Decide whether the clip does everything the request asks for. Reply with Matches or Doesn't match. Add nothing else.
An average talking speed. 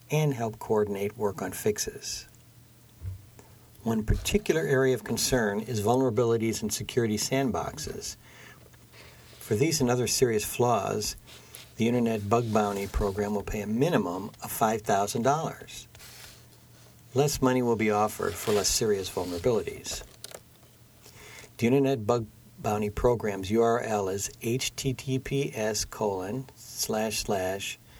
Doesn't match